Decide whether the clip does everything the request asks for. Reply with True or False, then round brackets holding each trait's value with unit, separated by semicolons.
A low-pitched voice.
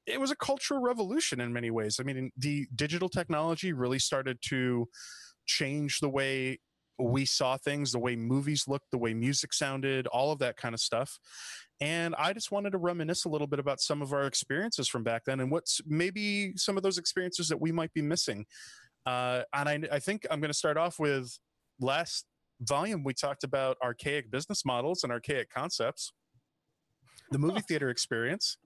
False (145 Hz)